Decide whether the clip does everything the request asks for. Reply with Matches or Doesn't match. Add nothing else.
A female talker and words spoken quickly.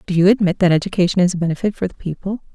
Matches